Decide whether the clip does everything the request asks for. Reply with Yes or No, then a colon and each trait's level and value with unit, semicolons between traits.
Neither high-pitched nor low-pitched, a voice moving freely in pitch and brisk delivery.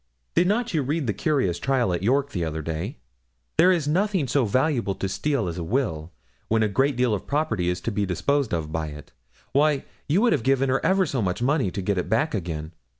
No: low, 120 Hz; wide, 8.2 semitones; fast, 230 wpm